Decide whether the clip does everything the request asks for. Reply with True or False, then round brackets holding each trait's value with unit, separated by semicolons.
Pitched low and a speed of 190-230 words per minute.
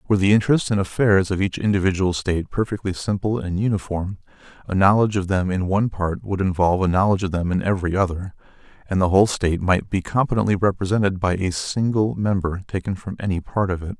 True (95 Hz; 200 wpm)